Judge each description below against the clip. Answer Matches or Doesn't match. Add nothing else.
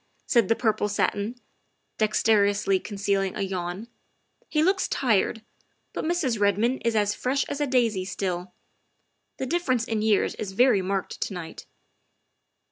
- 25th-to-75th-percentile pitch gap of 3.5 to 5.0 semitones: Matches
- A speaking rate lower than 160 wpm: Matches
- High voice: Matches